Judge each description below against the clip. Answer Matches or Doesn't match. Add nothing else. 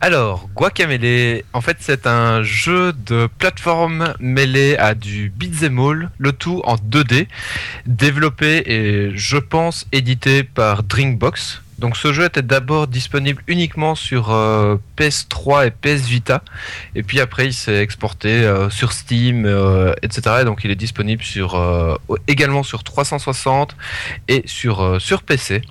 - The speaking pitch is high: Doesn't match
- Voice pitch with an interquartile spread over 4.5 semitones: Matches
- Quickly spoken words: Doesn't match